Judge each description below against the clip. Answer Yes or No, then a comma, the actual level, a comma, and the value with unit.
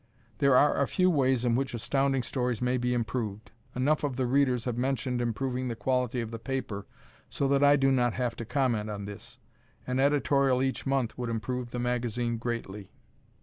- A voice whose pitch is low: Yes, low, 125 Hz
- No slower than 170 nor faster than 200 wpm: Yes, average, 190 wpm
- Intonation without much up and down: Yes, narrow, 2.3 semitones